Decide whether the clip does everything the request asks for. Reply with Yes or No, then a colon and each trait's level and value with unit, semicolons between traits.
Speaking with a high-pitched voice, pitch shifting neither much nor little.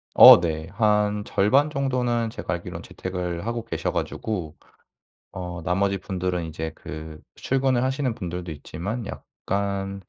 No: low, 100 Hz; average, 4.9 semitones